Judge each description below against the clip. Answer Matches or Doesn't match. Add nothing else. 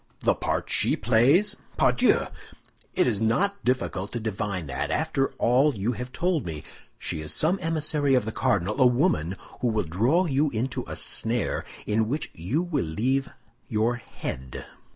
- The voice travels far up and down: Matches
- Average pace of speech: Matches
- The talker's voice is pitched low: Matches